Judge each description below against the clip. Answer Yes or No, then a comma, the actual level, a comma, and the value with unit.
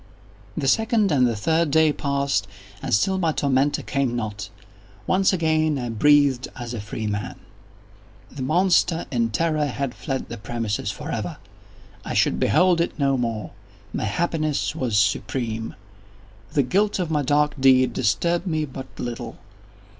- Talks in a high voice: No, medium, 140 Hz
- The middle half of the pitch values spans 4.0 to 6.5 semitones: Yes, average, 5.1 semitones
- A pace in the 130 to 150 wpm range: Yes, average, 145 wpm